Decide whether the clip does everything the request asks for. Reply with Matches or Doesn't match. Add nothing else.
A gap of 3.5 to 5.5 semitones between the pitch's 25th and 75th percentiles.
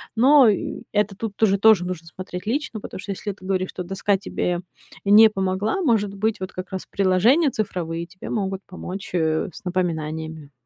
Doesn't match